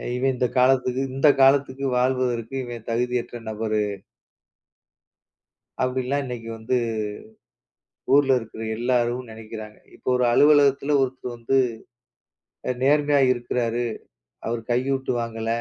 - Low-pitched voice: Yes, low, 125 Hz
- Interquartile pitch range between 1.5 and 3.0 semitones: Yes, narrow, 2.4 semitones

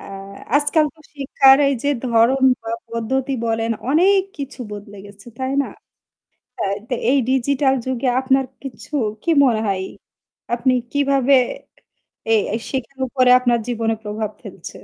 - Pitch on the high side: Yes, very high, 260 Hz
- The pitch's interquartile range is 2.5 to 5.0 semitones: Yes, average, 3.4 semitones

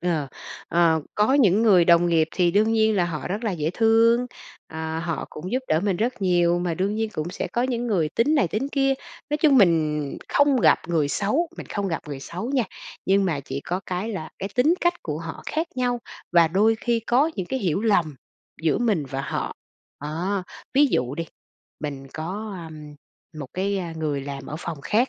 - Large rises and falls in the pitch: Yes, wide, 6.0 semitones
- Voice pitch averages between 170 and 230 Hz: Yes, medium, 185 Hz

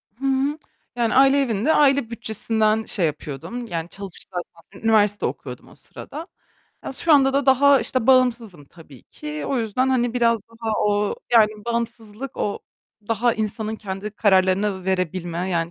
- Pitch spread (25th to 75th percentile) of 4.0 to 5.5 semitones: Yes, average, 4.8 semitones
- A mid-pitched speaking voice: No, high, 220 Hz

